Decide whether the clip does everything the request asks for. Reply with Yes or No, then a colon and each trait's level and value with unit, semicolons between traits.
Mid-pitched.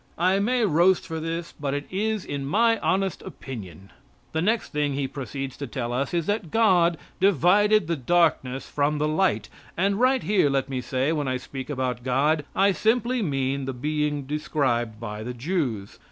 Yes: medium, 150 Hz